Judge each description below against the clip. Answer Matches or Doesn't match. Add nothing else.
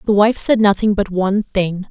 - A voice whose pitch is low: Doesn't match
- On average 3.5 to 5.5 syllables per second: Matches